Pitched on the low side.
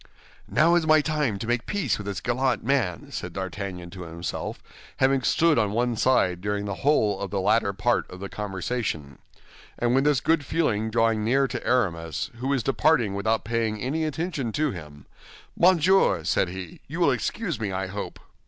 Yes: low, 110 Hz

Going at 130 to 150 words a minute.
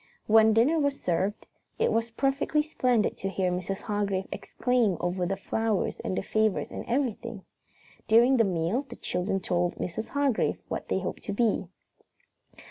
No: average, 160 wpm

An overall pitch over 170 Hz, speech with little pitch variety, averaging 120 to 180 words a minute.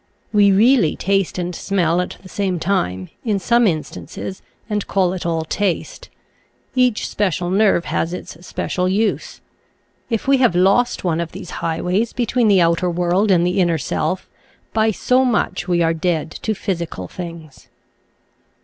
No: medium, 185 Hz; average, 3.6 semitones; average, 160 wpm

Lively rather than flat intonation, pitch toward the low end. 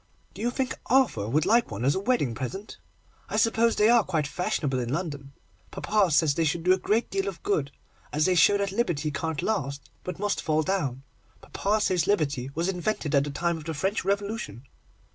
No: wide, 6.0 semitones; medium, 175 Hz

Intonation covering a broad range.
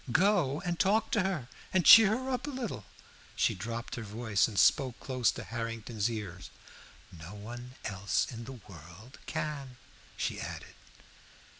Yes: wide, 8.2 semitones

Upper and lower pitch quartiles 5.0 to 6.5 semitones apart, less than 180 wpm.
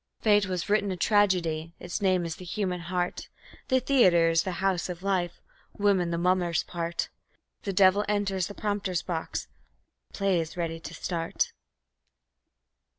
No: average, 2.7 semitones; average, 160 wpm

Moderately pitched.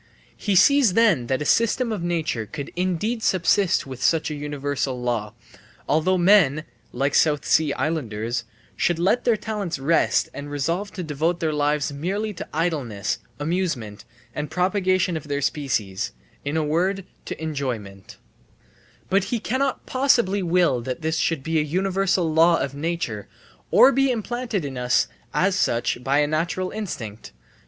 Yes: medium, 160 Hz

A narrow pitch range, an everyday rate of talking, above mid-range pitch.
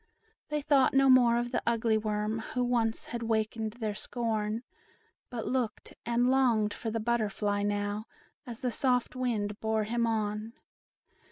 Yes: narrow, 2.2 semitones; average, 155 wpm; high, 225 Hz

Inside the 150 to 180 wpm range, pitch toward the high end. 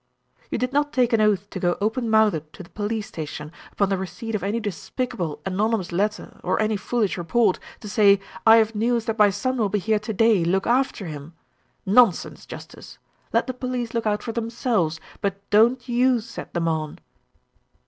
No: average, 190 wpm; high, 215 Hz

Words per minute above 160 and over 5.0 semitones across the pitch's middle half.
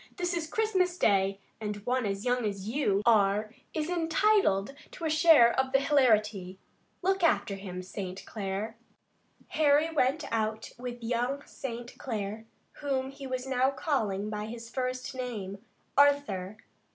No: average, 145 wpm; wide, 5.6 semitones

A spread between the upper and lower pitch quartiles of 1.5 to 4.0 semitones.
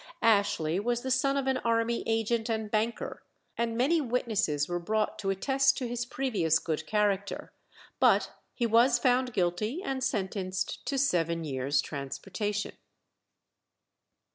No: average, 5.0 semitones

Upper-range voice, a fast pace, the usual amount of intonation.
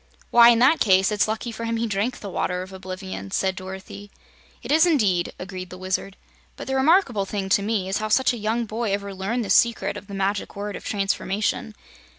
Yes: high, 205 Hz; fast, 215 wpm; average, 3.3 semitones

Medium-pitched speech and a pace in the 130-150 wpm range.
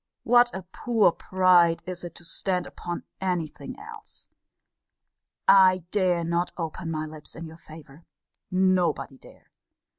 Yes: medium, 175 Hz; average, 140 wpm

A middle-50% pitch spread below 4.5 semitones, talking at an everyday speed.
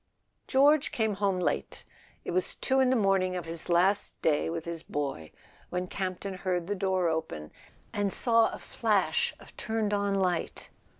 Yes: average, 3.2 semitones; average, 170 wpm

